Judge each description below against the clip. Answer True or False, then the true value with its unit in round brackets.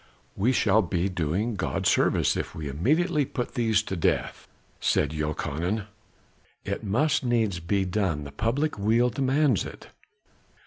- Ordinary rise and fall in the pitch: False (6.0 semitones)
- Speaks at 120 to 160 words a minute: True (140 wpm)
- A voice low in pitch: True (105 Hz)